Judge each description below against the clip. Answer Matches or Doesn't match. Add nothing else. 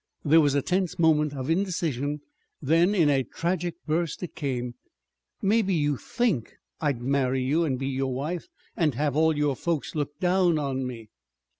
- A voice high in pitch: Doesn't match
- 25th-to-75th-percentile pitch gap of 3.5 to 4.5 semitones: Matches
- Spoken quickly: Doesn't match